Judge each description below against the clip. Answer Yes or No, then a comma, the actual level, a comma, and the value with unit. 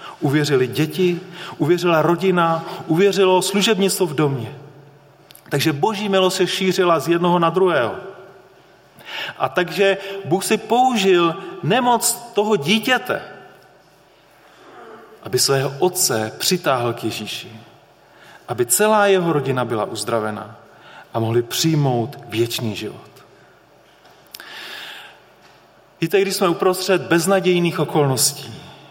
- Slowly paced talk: Yes, slow, 100 wpm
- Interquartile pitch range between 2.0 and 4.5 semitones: No, average, 5.0 semitones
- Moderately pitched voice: Yes, medium, 175 Hz